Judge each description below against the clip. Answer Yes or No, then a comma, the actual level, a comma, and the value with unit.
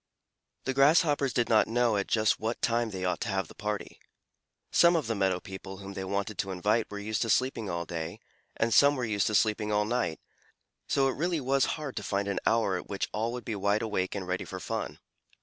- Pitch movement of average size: Yes, average, 3.8 semitones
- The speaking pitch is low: Yes, low, 105 Hz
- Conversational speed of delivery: No, fast, 230 wpm